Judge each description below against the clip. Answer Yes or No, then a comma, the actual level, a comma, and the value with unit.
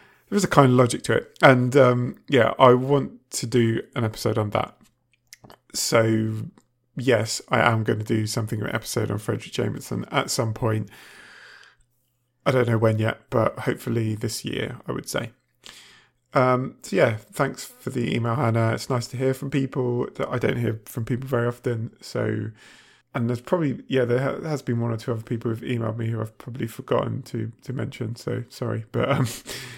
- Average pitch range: No, narrow, 2.0 semitones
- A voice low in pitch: Yes, low, 120 Hz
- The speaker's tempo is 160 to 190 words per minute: No, average, 200 wpm